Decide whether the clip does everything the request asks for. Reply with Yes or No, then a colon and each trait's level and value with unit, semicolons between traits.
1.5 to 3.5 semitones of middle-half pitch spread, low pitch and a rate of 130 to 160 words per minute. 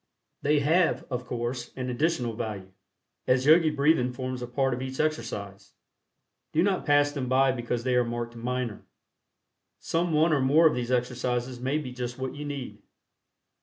No: average, 3.1 semitones; low, 130 Hz; average, 170 wpm